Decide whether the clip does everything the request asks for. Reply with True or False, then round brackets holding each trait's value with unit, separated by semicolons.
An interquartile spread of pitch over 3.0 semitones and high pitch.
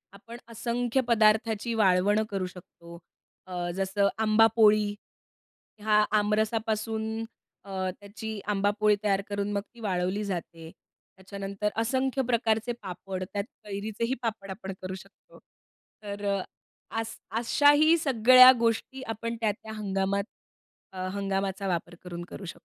False (2.5 semitones; 210 Hz)